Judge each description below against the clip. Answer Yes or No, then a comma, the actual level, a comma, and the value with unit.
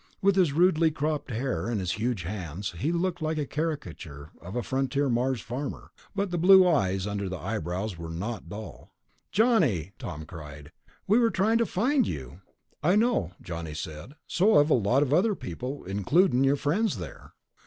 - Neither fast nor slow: Yes, average, 180 wpm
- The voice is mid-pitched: No, low, 130 Hz